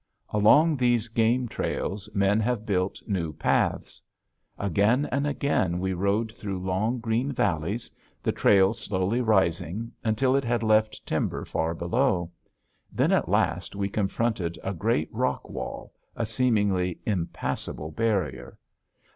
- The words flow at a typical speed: No, slow, 130 wpm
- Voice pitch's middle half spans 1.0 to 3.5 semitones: No, average, 3.9 semitones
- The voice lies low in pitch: Yes, low, 105 Hz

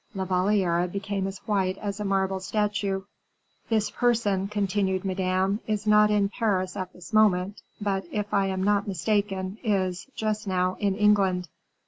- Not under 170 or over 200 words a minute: No, average, 155 wpm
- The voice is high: Yes, high, 195 Hz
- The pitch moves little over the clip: Yes, narrow, 1.8 semitones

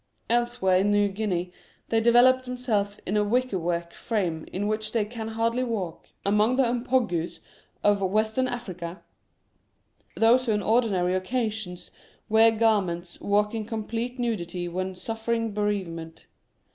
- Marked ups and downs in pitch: No, average, 3.9 semitones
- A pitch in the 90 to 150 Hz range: No, high, 215 Hz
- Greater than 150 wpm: No, slow, 135 wpm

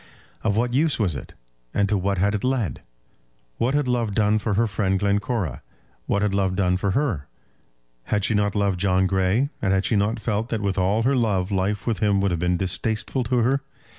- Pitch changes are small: No, average, 3.0 semitones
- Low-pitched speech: Yes, low, 100 Hz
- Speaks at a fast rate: Yes, fast, 215 wpm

